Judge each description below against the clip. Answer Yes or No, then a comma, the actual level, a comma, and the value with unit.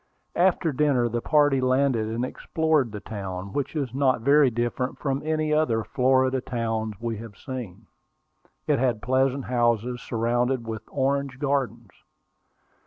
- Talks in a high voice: No, low, 125 Hz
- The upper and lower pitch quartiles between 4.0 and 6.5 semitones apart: No, average, 3.2 semitones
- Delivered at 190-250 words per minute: No, average, 140 wpm